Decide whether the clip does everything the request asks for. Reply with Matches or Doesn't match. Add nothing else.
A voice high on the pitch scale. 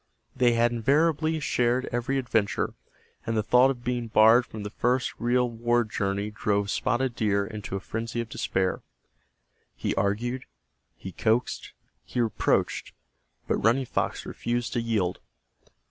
Doesn't match